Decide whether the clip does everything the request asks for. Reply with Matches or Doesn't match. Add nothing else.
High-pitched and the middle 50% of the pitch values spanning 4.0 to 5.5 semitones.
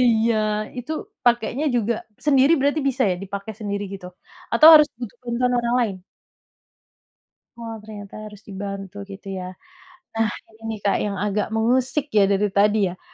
Doesn't match